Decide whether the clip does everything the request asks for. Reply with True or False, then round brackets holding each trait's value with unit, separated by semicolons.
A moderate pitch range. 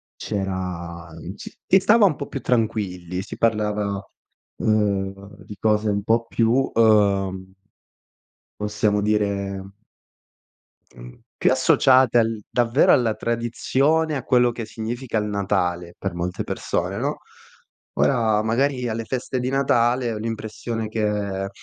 True (3.2 semitones)